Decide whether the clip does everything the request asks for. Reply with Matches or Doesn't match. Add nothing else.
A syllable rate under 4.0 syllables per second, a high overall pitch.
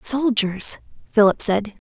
Matches